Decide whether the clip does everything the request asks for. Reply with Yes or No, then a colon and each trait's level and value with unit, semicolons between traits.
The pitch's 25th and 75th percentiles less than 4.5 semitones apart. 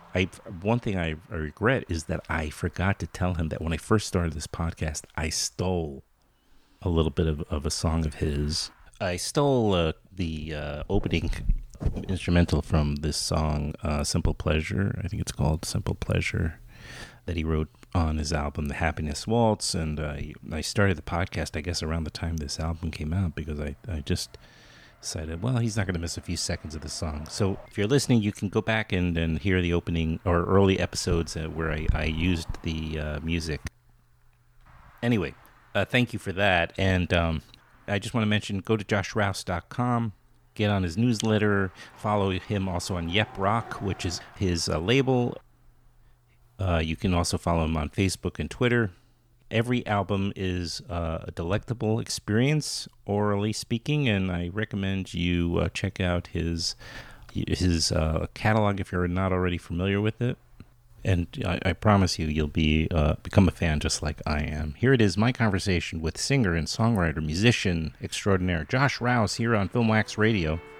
No: average, 4.9 semitones